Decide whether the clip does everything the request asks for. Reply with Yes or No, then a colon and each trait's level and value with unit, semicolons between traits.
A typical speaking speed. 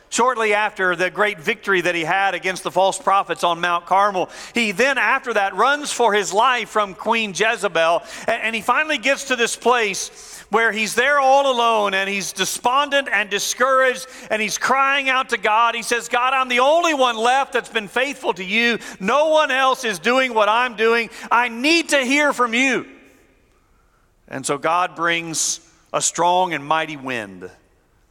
Yes: average, 180 wpm